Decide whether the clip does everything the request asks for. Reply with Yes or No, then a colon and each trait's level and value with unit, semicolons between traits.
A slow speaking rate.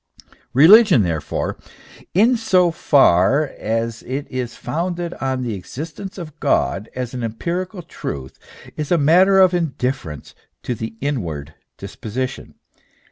Yes: slow, 125 wpm